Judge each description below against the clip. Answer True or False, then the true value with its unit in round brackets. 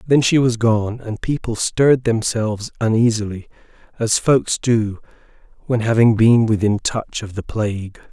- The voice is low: True (115 Hz)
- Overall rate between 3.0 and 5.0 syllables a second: True (4.5 syllables/s)